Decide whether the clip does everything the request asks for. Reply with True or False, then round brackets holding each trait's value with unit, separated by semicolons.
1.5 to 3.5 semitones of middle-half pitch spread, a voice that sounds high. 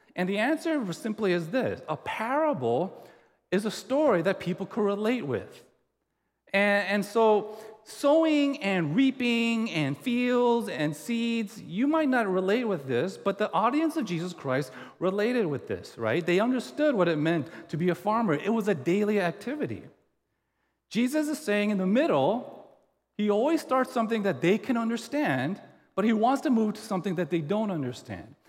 False (4.9 semitones; 215 Hz)